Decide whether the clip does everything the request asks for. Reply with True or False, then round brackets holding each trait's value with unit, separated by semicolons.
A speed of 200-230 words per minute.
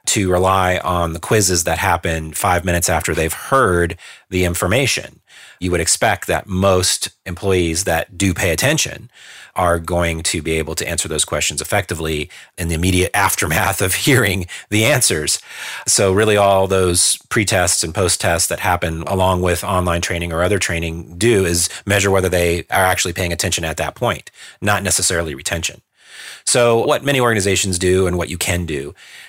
False (175 wpm)